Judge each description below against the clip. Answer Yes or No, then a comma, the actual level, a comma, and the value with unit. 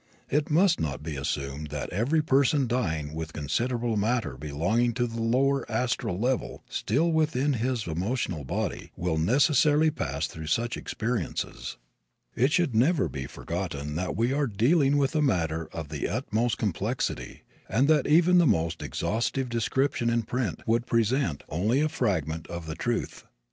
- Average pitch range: No, wide, 8.5 semitones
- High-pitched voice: No, low, 115 Hz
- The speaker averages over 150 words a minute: Yes, average, 160 wpm